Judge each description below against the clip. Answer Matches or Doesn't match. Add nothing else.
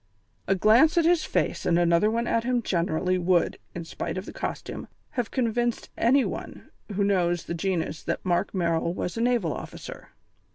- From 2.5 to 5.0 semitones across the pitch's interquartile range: Doesn't match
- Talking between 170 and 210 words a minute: Matches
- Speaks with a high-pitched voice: Matches